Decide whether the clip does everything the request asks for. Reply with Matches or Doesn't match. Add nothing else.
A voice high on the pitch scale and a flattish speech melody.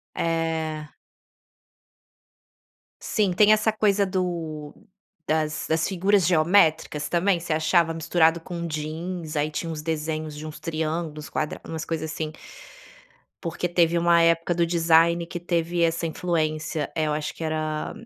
Doesn't match